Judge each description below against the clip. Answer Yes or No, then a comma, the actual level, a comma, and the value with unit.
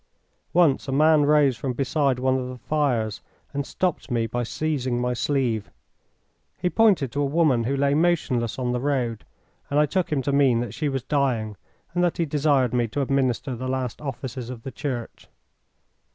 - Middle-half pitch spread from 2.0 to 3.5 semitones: Yes, average, 3.1 semitones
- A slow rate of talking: No, average, 190 wpm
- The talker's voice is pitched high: No, low, 135 Hz